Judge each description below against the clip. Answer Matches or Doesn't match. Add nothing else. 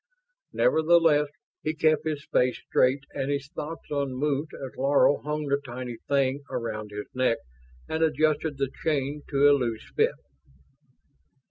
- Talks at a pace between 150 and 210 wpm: Doesn't match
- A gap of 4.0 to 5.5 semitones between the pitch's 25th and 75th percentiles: Doesn't match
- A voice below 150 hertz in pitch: Matches